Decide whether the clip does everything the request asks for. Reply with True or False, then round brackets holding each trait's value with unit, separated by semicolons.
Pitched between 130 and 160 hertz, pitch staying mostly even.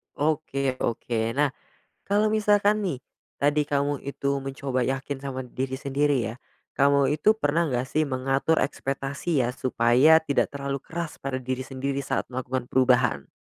True (140 Hz; 2.3 semitones)